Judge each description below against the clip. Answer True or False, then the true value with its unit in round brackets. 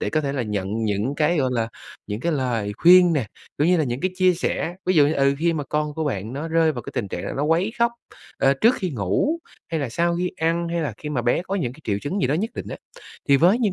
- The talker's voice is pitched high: False (150 Hz)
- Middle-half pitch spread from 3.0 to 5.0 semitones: False (5.4 semitones)